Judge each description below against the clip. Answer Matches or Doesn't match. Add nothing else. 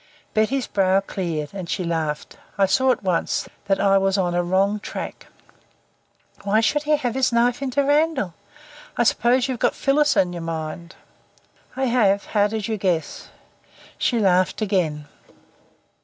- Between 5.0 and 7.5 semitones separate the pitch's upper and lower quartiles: Matches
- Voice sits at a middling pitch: Doesn't match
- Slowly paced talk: Doesn't match